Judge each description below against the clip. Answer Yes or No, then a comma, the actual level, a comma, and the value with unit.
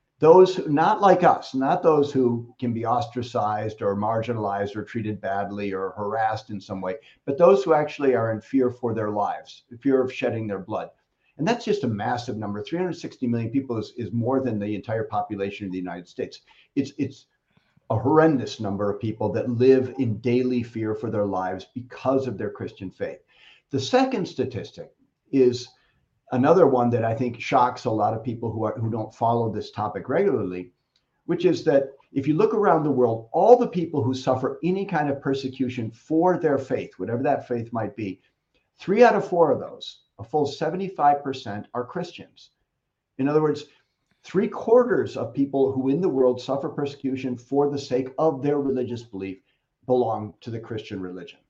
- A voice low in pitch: Yes, low, 125 Hz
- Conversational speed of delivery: Yes, average, 185 wpm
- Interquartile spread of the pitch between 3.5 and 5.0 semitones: Yes, average, 4.5 semitones